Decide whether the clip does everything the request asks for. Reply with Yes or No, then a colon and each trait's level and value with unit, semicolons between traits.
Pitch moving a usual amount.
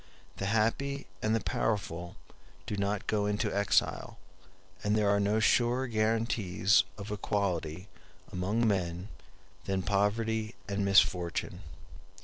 No: narrow, 2.2 semitones